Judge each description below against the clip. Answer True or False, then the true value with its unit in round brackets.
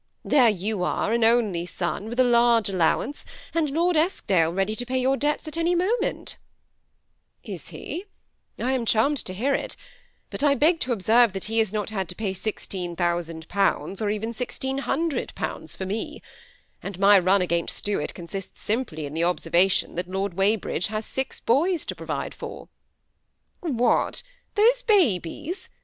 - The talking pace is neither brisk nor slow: True (170 wpm)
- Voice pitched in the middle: False (220 Hz)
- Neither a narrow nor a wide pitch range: False (6.3 semitones)